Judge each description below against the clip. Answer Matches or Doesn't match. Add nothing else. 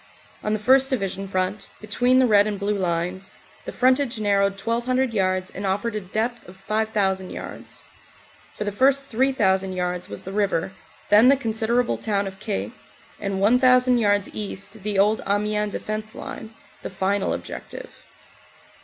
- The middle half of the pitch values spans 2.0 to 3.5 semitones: Matches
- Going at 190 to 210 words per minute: Doesn't match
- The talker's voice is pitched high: Matches